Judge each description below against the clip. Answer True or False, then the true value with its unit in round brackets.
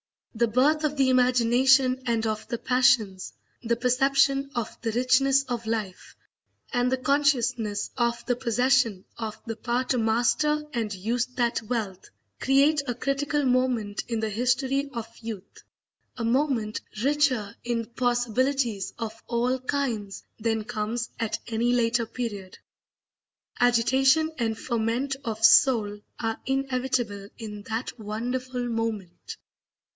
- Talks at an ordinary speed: False (130 wpm)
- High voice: True (240 Hz)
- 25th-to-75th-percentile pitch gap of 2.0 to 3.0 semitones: True (2.6 semitones)